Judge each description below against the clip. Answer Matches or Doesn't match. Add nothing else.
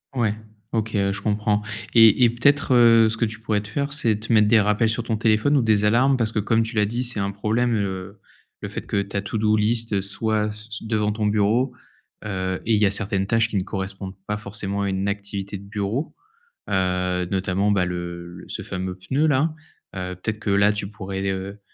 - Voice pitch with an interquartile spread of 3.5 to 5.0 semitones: Doesn't match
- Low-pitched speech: Matches